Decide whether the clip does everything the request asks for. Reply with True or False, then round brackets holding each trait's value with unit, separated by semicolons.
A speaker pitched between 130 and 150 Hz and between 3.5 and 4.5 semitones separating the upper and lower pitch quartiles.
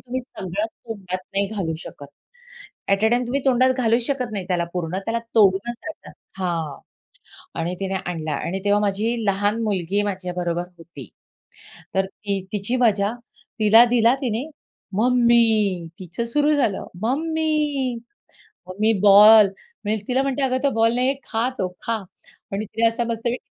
False (215 Hz; 4.0 semitones)